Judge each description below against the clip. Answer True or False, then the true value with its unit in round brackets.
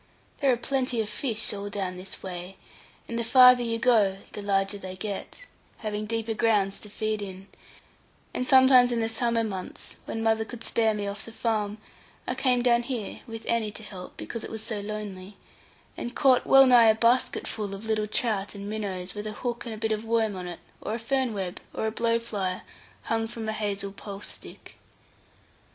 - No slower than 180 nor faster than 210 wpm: True (200 wpm)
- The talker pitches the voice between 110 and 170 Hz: False (220 Hz)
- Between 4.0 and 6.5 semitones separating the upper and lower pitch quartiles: False (2.5 semitones)